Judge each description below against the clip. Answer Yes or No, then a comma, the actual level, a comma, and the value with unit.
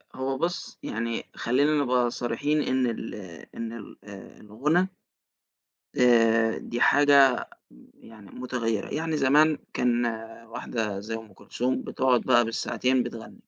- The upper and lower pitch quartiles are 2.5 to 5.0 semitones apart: Yes, average, 2.8 semitones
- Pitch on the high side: No, low, 120 Hz